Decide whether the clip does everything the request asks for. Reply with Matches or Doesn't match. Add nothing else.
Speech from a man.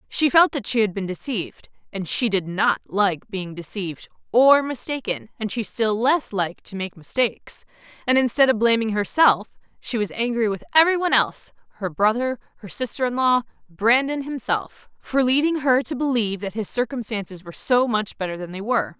Doesn't match